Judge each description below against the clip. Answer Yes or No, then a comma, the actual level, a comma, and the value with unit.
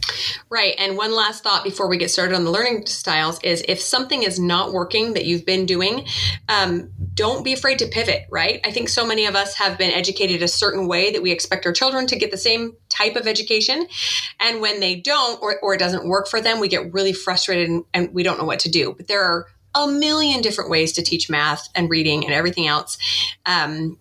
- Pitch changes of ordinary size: Yes, average, 4.0 semitones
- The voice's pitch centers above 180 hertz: Yes, high, 190 Hz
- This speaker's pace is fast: Yes, fast, 230 wpm